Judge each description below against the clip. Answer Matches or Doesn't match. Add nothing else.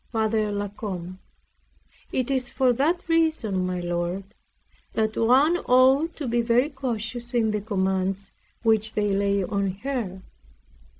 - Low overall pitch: Doesn't match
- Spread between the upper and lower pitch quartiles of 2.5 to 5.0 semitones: Matches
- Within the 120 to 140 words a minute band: Matches